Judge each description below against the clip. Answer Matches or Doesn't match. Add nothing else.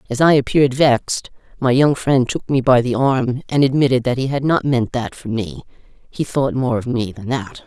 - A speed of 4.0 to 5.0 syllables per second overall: Matches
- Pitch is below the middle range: Matches